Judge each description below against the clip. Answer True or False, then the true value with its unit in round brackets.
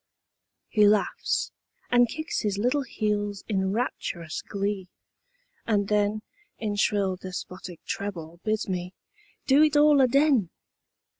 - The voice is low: False (205 Hz)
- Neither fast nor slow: False (120 wpm)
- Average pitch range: True (4.2 semitones)